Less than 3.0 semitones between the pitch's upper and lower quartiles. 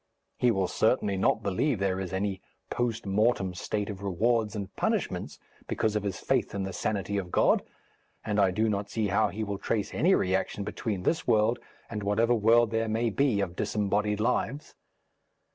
Yes: narrow, 2.4 semitones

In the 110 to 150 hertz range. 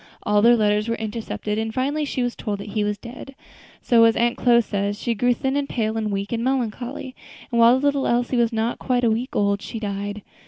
No: high, 230 Hz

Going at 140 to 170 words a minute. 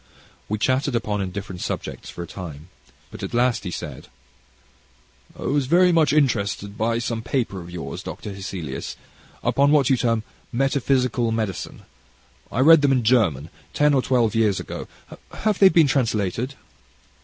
Yes: average, 155 wpm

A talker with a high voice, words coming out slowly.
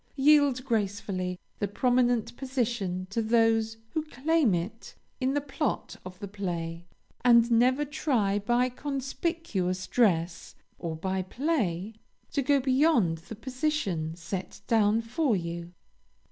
Yes: high, 225 Hz; slow, 125 wpm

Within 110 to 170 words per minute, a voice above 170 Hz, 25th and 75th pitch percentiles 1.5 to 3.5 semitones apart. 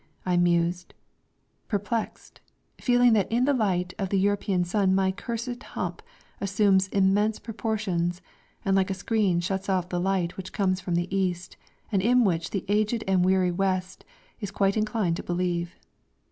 Yes: average, 160 wpm; high, 190 Hz; average, 2.8 semitones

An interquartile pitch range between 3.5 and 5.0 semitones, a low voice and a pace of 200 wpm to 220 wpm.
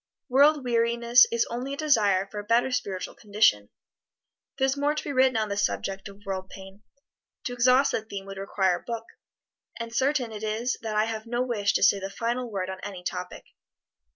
No: average, 3.9 semitones; high, 225 Hz; fast, 205 wpm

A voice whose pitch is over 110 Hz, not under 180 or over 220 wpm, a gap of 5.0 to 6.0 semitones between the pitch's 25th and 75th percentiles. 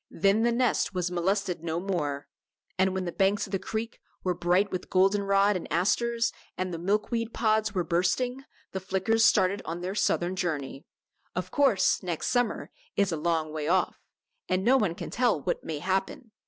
No: high, 190 Hz; average, 190 wpm; average, 3.5 semitones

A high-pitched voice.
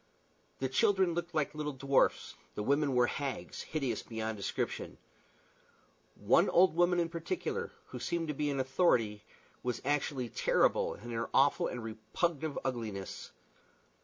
No: medium, 140 Hz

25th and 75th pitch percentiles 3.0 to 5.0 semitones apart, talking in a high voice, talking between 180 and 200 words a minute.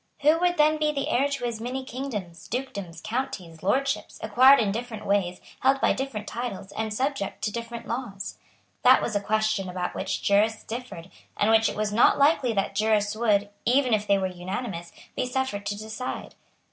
Yes: average, 4.3 semitones; high, 220 Hz; average, 185 wpm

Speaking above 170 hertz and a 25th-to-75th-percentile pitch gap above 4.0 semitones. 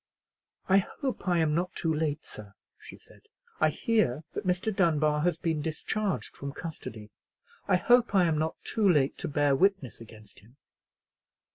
No: medium, 160 Hz; average, 4.8 semitones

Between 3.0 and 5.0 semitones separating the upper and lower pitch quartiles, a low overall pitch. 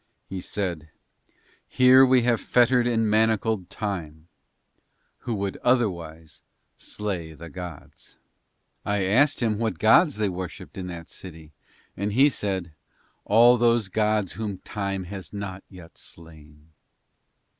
Yes: average, 4.4 semitones; low, 100 Hz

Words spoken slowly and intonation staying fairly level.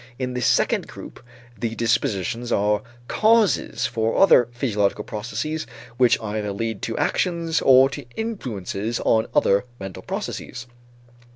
No: slow, 125 wpm; average, 4.1 semitones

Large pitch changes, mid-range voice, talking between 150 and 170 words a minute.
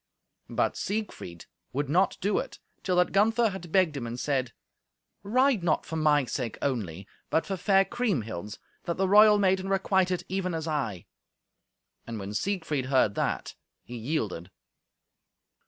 Yes: wide, 7.8 semitones; medium, 160 Hz; average, 155 wpm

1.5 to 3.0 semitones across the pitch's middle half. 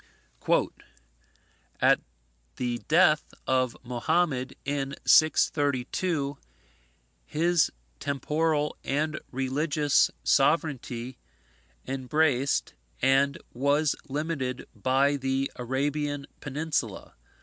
Yes: narrow, 2.6 semitones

